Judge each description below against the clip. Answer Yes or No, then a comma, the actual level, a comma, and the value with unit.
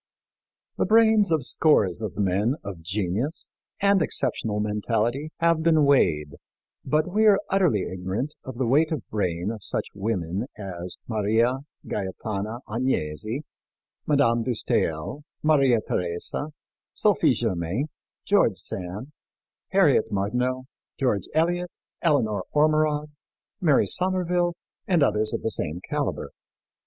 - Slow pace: Yes, slow, 120 wpm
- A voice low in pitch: Yes, low, 120 Hz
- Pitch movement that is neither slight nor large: No, wide, 7.4 semitones